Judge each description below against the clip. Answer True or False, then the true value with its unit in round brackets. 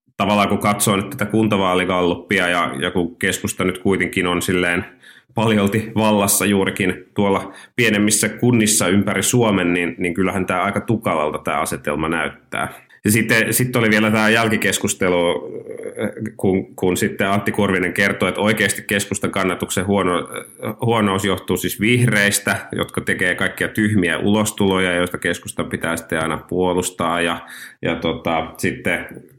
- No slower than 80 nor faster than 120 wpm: False (140 wpm)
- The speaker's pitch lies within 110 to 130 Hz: False (100 Hz)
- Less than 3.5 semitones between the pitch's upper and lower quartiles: True (2.8 semitones)